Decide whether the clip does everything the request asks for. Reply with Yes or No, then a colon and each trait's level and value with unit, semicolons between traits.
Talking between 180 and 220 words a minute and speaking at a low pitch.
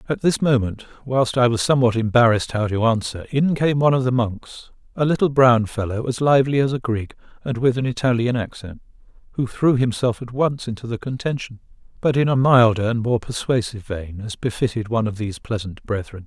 Yes: average, 200 wpm; low, 120 Hz